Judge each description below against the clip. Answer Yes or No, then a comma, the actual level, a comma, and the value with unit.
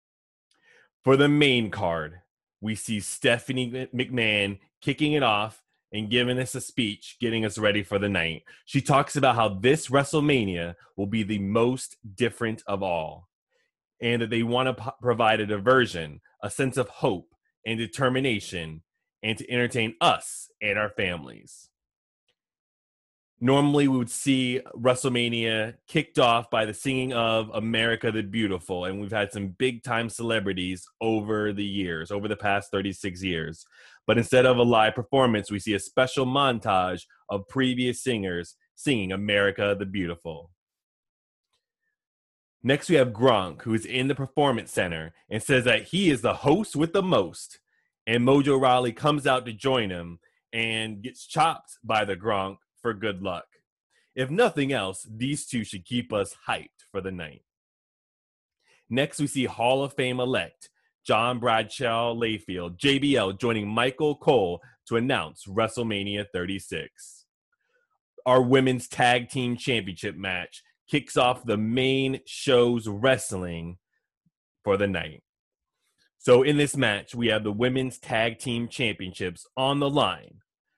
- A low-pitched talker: Yes, low, 115 Hz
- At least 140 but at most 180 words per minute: Yes, average, 150 wpm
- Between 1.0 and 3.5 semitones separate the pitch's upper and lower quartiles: No, average, 4.3 semitones